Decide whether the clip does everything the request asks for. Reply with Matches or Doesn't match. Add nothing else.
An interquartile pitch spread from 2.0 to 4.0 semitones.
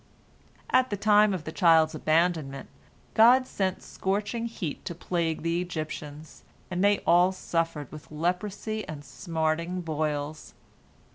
Matches